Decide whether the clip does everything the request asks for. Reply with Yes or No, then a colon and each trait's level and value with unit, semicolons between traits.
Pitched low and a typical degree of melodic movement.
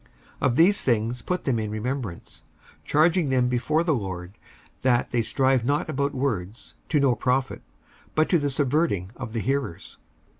Yes: low, 130 Hz; average, 4.0 semitones